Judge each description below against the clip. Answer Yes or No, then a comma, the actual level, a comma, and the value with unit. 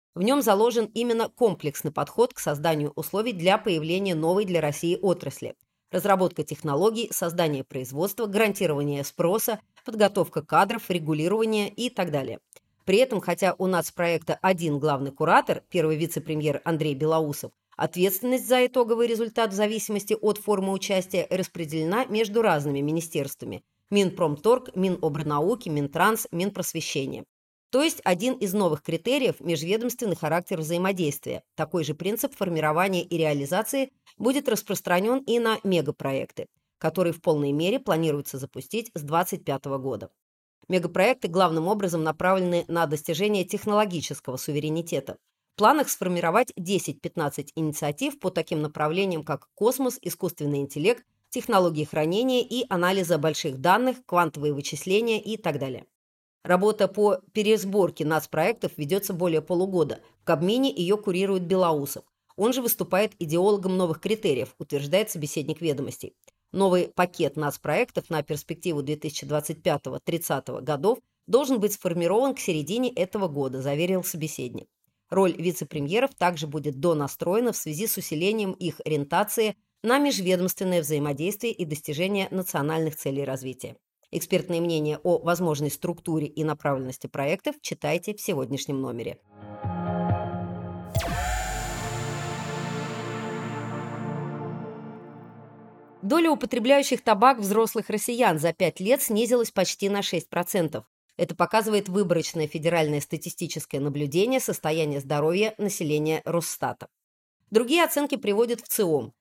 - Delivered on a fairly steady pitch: No, average, 5.2 semitones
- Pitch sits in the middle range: Yes, medium, 175 Hz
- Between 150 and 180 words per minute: No, average, 115 wpm